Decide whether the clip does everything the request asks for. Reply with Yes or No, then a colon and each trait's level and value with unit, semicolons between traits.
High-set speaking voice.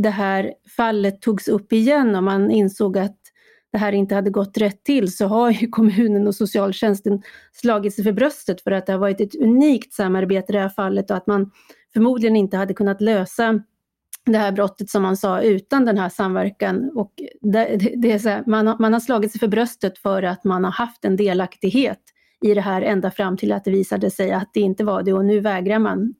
Yes: high, 205 Hz